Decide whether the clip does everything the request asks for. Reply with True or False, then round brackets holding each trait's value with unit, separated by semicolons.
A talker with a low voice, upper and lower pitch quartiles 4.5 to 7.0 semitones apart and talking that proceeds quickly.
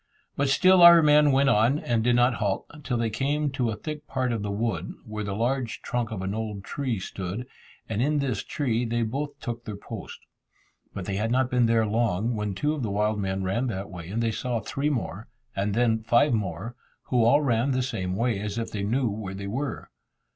False (115 Hz; 3.9 semitones; 225 wpm)